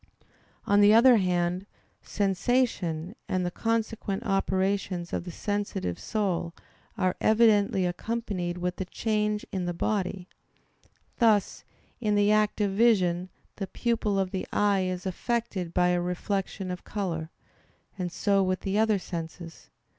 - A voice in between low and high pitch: No, high, 195 Hz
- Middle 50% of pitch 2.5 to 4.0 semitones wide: Yes, average, 2.8 semitones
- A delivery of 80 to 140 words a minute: Yes, slow, 135 wpm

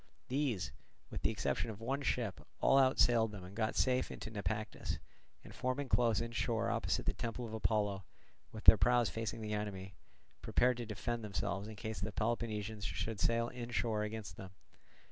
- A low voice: Yes, low, 110 Hz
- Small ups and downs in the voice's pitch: Yes, narrow, 2.1 semitones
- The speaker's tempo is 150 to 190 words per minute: Yes, average, 170 wpm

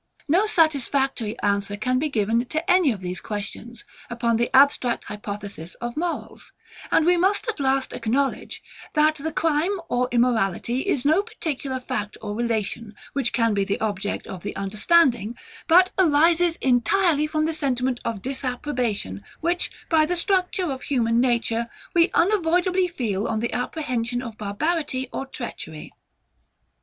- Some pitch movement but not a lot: No, wide, 6.1 semitones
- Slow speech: No, average, 150 wpm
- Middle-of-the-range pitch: No, very high, 255 Hz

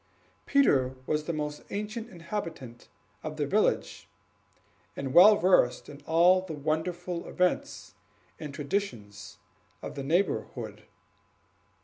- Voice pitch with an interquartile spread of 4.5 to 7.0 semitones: Yes, average, 5.1 semitones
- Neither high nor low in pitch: Yes, medium, 160 Hz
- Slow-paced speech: Yes, slow, 110 wpm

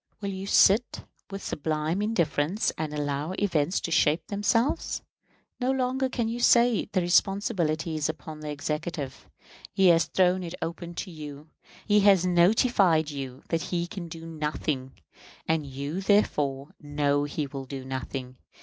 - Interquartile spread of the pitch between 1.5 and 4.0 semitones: No, average, 4.9 semitones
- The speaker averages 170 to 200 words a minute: No, average, 150 wpm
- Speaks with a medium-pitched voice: Yes, medium, 165 Hz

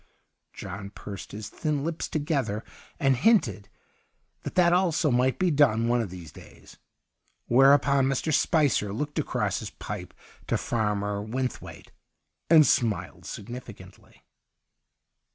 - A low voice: Yes, low, 125 Hz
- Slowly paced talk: Yes, slow, 120 wpm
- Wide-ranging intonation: Yes, wide, 6.1 semitones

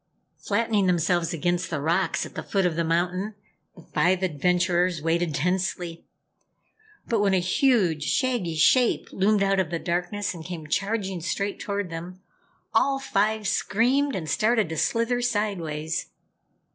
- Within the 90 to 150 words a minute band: Yes, average, 145 wpm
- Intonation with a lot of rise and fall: No, average, 3.6 semitones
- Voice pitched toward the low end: No, medium, 185 Hz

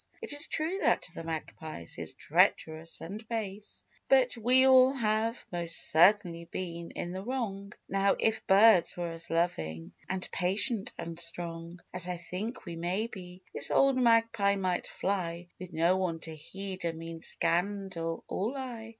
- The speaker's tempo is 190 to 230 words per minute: No, average, 160 wpm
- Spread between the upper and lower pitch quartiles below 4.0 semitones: No, average, 4.7 semitones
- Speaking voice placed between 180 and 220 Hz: Yes, medium, 185 Hz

